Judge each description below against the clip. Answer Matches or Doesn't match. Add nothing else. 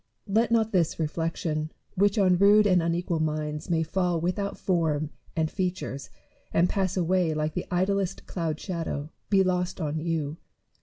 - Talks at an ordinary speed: Matches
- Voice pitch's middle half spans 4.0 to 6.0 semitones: Doesn't match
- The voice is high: Doesn't match